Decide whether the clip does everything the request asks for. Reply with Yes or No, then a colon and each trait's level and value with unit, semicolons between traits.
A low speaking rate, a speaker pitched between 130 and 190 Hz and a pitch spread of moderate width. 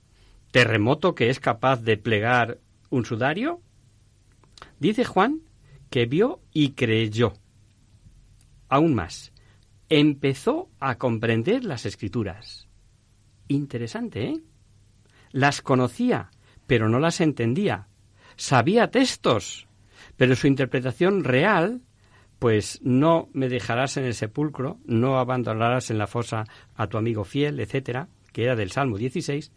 No: slow, 115 wpm; low, 120 Hz; average, 4.2 semitones